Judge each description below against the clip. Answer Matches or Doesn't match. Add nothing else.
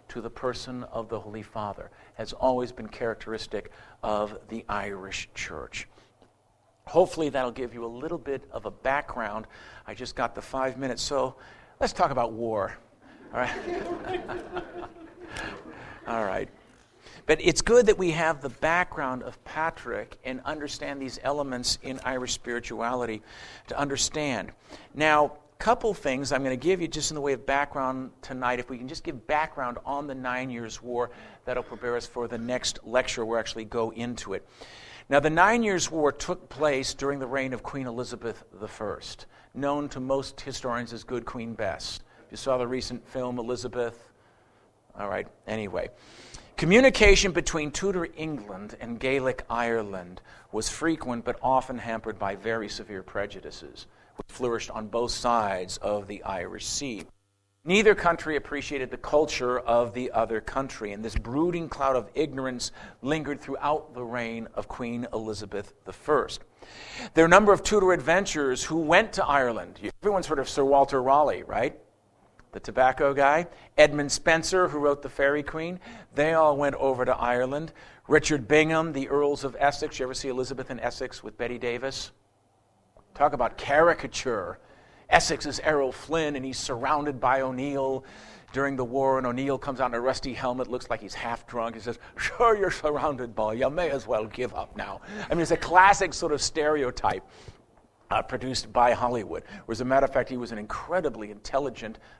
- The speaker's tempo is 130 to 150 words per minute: Doesn't match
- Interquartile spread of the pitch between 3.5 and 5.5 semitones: Matches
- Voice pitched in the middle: Doesn't match